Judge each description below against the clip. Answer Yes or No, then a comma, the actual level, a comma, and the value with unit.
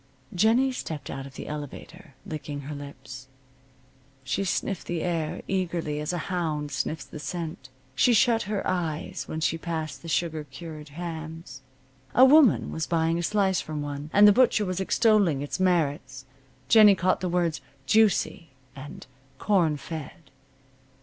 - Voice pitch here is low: No, medium, 165 Hz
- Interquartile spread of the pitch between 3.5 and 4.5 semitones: Yes, average, 4.1 semitones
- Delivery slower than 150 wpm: No, average, 155 wpm